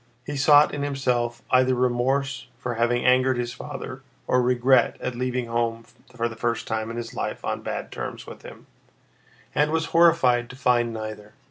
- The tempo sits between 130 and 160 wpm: No, average, 175 wpm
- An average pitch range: No, narrow, 2.0 semitones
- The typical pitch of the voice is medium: No, low, 125 Hz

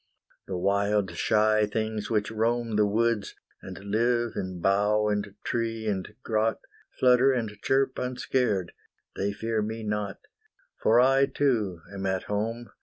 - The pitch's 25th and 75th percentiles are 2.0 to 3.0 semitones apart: Yes, narrow, 2.4 semitones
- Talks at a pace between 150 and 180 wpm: No, average, 140 wpm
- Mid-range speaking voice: No, low, 110 Hz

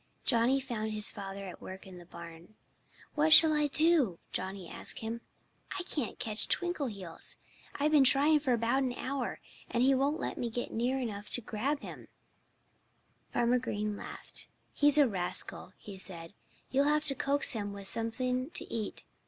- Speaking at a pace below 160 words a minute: No, average, 175 wpm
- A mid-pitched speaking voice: No, high, 240 Hz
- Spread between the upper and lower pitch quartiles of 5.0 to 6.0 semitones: Yes, wide, 5.4 semitones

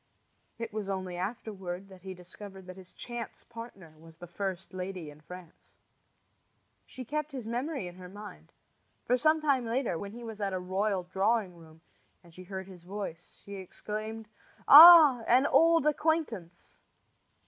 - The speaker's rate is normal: Yes, average, 160 wpm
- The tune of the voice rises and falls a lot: No, average, 4.7 semitones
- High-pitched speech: Yes, high, 195 Hz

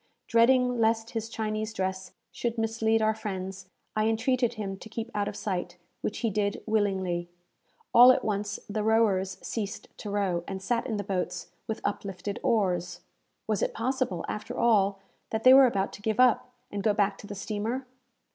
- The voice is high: Yes, high, 215 Hz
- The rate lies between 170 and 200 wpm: Yes, average, 180 wpm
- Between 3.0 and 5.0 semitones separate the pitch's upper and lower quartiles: No, narrow, 2.6 semitones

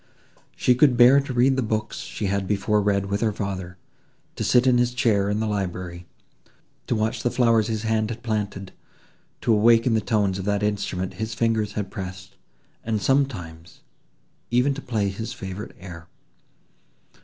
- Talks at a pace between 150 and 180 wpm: Yes, average, 165 wpm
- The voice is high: No, low, 105 Hz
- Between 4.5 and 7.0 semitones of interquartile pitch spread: No, average, 3.2 semitones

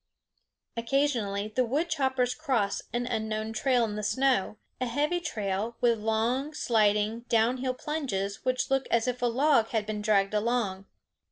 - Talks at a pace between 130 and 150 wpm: No, average, 160 wpm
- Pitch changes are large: No, average, 3.5 semitones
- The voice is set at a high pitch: Yes, high, 235 Hz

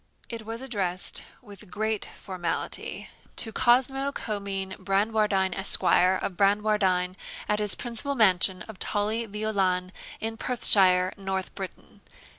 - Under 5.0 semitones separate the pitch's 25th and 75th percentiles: Yes, average, 2.7 semitones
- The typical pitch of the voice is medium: No, high, 205 Hz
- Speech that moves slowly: Yes, slow, 115 wpm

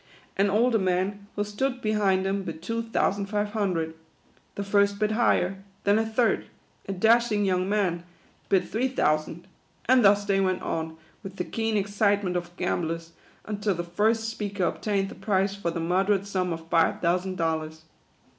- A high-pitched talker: Yes, high, 195 Hz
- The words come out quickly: No, average, 175 wpm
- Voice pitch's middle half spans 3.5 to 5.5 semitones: No, average, 2.8 semitones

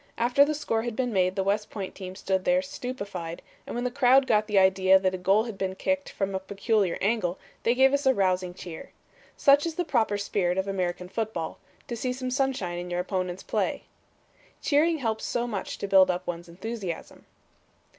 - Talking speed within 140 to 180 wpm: No, fast, 205 wpm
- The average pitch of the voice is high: Yes, high, 200 Hz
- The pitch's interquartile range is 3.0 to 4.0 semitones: No, average, 5.0 semitones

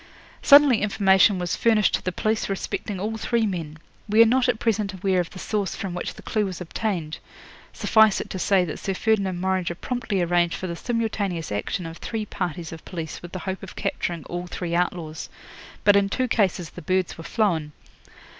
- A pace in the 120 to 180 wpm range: No, average, 200 wpm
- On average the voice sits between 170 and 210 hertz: Yes, high, 190 Hz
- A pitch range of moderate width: Yes, average, 3.6 semitones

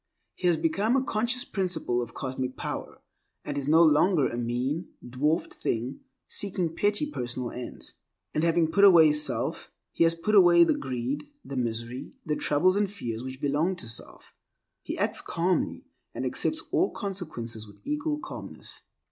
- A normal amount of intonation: No, wide, 6.9 semitones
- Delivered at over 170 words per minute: No, average, 165 wpm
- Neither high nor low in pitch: Yes, medium, 160 Hz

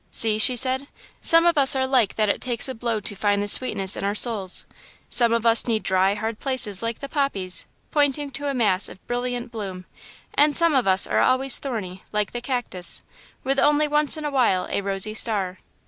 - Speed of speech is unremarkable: No, fast, 215 wpm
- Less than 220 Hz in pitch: No, high, 235 Hz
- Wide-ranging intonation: No, average, 4.8 semitones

